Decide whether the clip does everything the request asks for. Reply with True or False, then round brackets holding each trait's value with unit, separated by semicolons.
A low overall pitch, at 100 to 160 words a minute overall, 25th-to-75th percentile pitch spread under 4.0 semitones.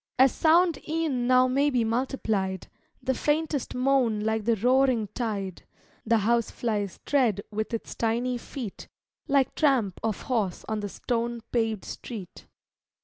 False (235 Hz; 140 wpm; 3.4 semitones)